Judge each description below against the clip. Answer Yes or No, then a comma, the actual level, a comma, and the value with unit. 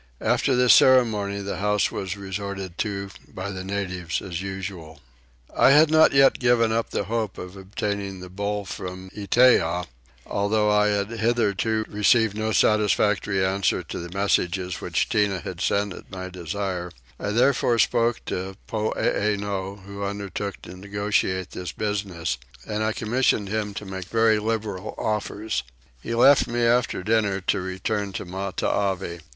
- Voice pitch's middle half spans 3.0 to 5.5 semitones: No, narrow, 2.4 semitones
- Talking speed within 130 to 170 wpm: Yes, average, 150 wpm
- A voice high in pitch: No, low, 100 Hz